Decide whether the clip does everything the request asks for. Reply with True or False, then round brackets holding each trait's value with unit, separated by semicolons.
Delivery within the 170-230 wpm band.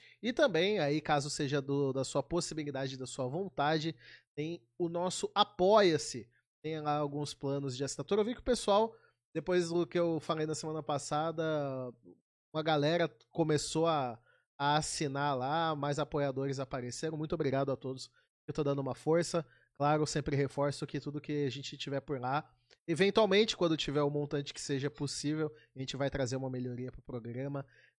True (180 wpm)